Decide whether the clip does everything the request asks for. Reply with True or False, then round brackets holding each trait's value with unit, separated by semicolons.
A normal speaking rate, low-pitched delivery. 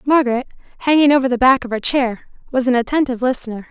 False (195 wpm; 255 Hz)